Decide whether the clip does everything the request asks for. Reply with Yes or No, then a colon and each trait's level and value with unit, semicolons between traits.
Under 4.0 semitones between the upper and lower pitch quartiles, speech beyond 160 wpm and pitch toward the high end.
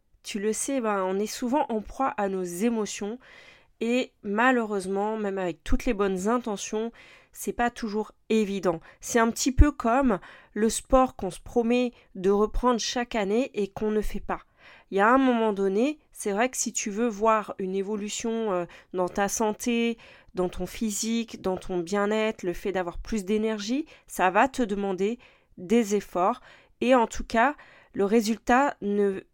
Yes: average, 3.1 semitones; average, 175 wpm; high, 220 Hz